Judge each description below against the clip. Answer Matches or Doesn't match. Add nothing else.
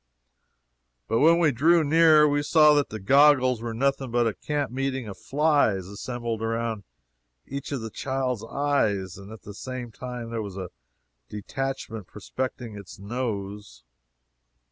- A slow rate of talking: Doesn't match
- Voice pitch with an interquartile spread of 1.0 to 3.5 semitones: Doesn't match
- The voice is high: Doesn't match